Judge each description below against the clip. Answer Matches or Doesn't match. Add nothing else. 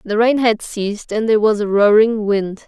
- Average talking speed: Doesn't match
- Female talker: Matches